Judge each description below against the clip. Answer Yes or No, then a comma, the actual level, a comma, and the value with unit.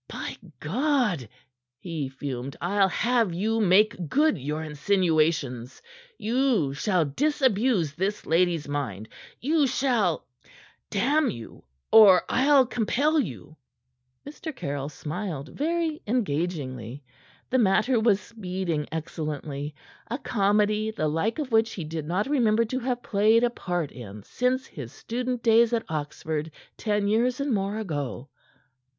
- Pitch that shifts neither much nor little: No, wide, 7.8 semitones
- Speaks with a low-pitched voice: No, high, 200 Hz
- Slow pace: Yes, slow, 130 wpm